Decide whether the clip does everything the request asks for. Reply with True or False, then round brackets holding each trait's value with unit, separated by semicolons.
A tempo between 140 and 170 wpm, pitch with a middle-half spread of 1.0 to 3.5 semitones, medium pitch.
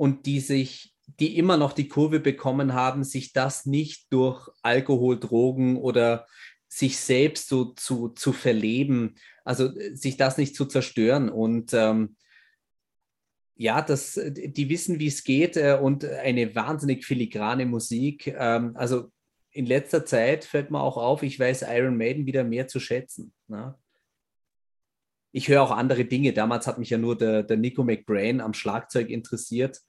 False (155 wpm; 2.6 semitones; 130 Hz)